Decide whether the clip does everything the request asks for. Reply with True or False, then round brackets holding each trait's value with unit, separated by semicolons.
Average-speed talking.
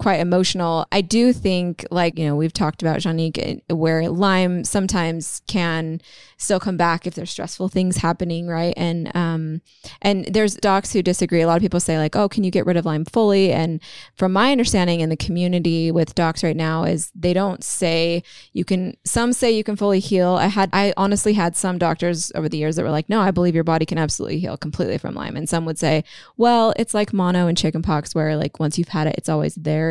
False (225 wpm)